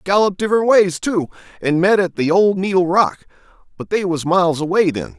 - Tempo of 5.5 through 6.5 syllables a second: Yes, 5.6 syllables/s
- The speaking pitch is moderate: Yes, medium, 180 Hz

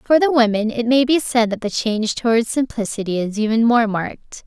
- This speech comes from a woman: Yes, female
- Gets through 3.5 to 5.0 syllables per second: No, 5.5 syllables/s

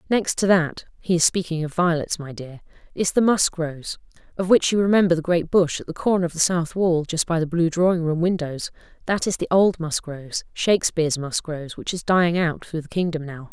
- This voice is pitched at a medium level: Yes, medium, 170 Hz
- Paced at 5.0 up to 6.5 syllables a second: Yes, 5.4 syllables/s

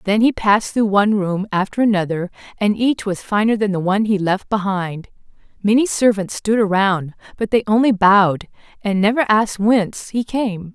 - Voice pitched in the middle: No, high, 205 Hz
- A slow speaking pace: No, average, 180 wpm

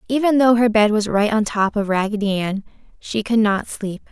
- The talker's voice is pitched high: Yes, high, 215 Hz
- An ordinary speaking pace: No, fast, 220 wpm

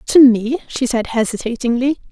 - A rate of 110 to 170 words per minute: Yes, average, 140 wpm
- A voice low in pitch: No, high, 245 Hz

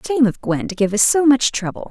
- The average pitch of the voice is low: No, high, 240 Hz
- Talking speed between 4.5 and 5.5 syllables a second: No, 6.3 syllables/s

